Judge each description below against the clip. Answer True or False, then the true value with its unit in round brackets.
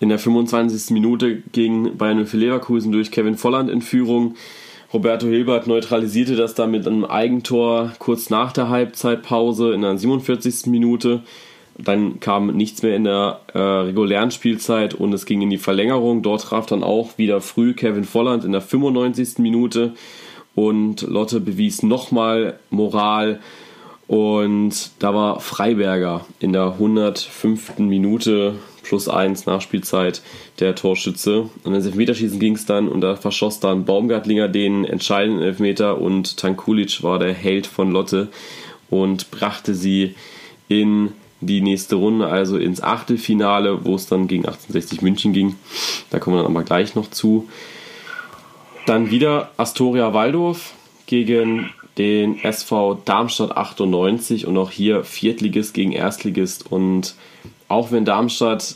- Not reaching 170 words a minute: True (140 wpm)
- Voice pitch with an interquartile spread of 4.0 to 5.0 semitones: False (2.7 semitones)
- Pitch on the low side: True (110 Hz)